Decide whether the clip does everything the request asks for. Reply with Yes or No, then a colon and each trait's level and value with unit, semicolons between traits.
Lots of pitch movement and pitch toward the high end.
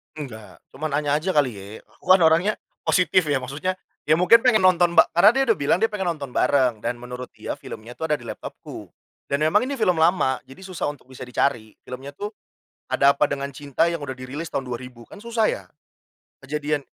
No: wide, 5.7 semitones; medium, 145 Hz